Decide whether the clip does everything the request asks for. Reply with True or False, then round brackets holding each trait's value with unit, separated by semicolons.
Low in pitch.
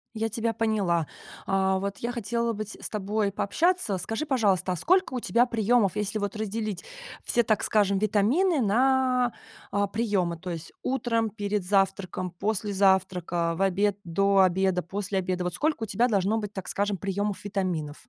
False (205 Hz)